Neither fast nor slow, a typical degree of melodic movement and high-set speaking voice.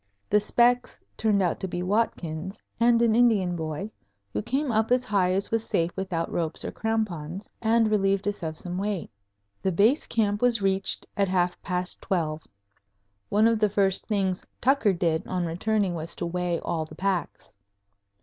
Yes: average, 175 wpm; average, 3.8 semitones; high, 195 Hz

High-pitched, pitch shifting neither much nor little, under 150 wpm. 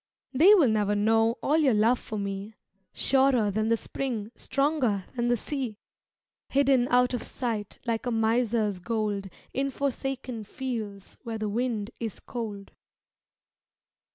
Yes: high, 230 Hz; average, 3.3 semitones; average, 140 wpm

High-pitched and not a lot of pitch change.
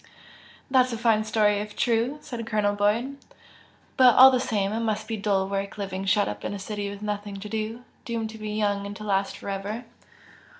Yes: high, 210 Hz; narrow, 2.0 semitones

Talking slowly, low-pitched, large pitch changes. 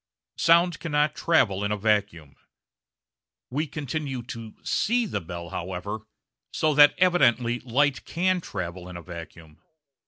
Yes: slow, 130 wpm; low, 120 Hz; wide, 8.6 semitones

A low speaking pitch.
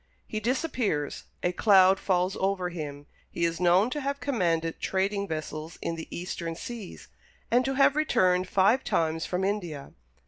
No: medium, 185 Hz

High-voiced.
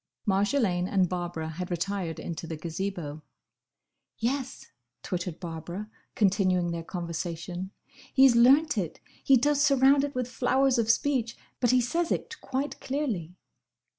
Yes: high, 200 Hz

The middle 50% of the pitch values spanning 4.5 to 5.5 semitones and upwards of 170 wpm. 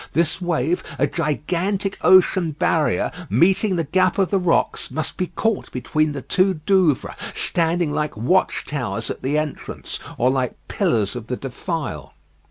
No: average, 5.2 semitones; average, 155 wpm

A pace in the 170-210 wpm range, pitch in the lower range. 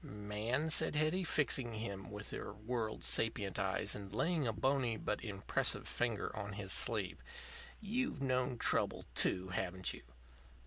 No: average, 145 wpm; low, 110 Hz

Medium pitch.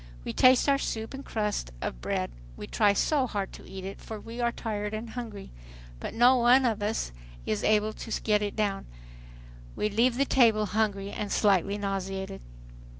No: high, 215 Hz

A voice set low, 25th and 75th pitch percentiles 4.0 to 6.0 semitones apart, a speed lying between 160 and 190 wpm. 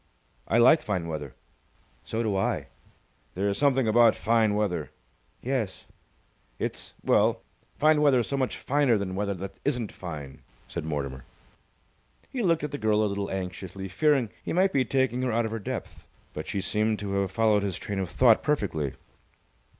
Yes: low, 110 Hz; average, 5.2 semitones; average, 175 wpm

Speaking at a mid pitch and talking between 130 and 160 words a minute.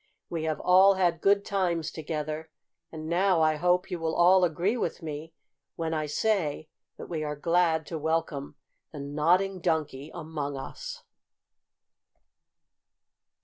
Yes: medium, 160 Hz; average, 140 wpm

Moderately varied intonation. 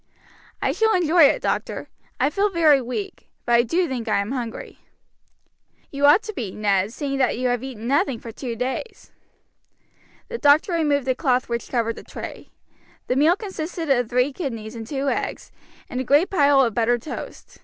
Yes: average, 4.7 semitones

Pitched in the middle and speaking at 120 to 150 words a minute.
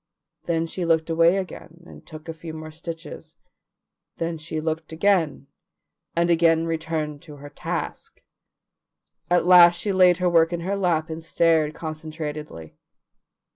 Yes: medium, 165 Hz; average, 145 wpm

